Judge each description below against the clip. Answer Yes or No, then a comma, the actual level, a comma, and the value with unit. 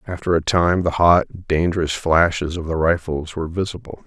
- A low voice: Yes, very low, 85 Hz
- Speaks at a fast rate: No, average, 175 wpm